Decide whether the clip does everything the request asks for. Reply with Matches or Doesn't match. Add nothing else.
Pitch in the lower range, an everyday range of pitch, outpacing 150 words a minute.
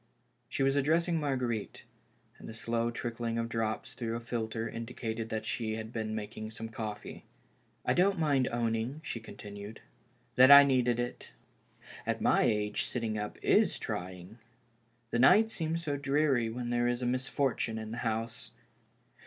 Matches